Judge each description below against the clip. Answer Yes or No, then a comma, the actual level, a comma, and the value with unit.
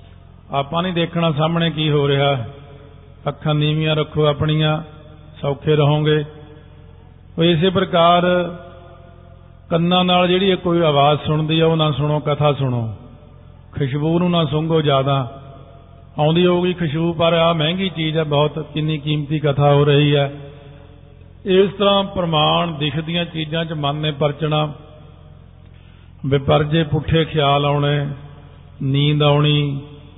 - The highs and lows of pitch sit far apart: No, average, 2.8 semitones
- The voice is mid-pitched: Yes, medium, 150 Hz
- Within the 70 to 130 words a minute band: Yes, average, 120 wpm